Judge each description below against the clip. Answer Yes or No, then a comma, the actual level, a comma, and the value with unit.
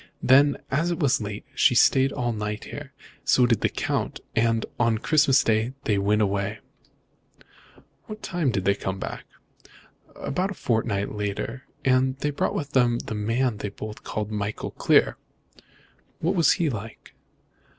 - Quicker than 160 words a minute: No, average, 155 wpm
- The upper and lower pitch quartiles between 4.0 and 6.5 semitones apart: Yes, average, 4.4 semitones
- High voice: No, low, 115 Hz